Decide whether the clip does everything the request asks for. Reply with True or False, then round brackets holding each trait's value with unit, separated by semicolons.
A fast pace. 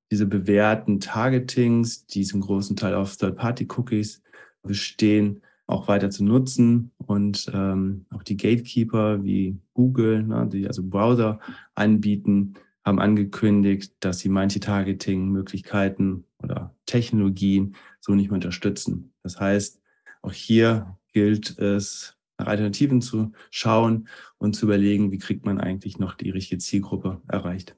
False (130 wpm)